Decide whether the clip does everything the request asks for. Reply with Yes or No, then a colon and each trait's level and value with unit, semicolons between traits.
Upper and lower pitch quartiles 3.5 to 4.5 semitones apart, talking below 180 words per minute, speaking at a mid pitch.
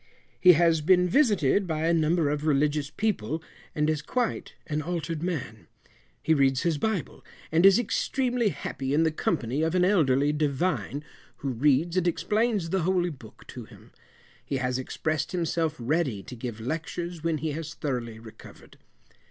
Yes: average, 4.0 semitones; average, 165 wpm; medium, 155 Hz